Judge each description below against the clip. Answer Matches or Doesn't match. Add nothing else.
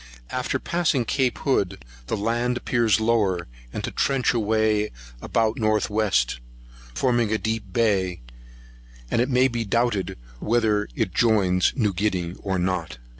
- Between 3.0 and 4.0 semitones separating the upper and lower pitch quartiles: Matches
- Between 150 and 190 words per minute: Doesn't match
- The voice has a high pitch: Doesn't match